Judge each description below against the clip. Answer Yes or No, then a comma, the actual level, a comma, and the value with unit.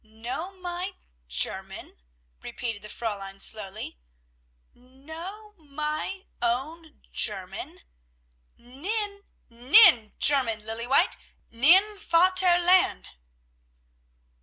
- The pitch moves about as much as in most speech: No, wide, 8.0 semitones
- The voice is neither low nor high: No, very high, 285 Hz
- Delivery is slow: Yes, slow, 85 wpm